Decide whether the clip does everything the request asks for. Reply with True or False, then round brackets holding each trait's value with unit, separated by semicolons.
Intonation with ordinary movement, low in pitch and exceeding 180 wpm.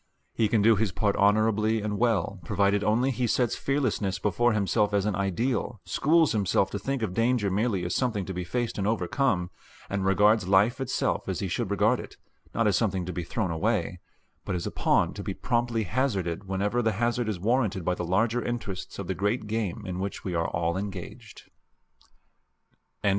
True (3.6 semitones; 105 Hz; 195 wpm)